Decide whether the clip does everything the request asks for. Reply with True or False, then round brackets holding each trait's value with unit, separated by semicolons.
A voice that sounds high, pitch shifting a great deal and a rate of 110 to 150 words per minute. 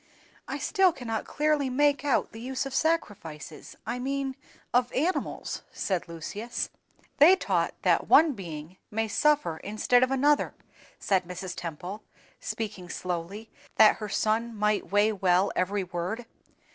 True (220 Hz; 6.5 semitones; 135 wpm)